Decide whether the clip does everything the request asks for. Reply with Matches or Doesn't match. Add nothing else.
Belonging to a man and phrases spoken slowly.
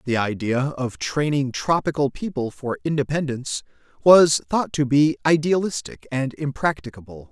Matches